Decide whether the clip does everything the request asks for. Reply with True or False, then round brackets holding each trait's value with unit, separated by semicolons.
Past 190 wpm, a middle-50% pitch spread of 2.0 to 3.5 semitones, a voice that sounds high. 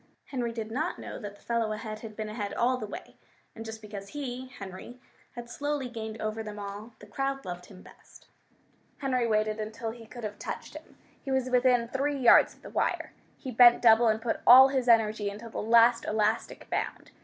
True (205 wpm; 2.7 semitones; 230 Hz)